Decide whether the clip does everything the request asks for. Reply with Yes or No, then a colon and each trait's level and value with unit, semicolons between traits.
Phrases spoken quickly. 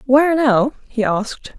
No: average, 150 wpm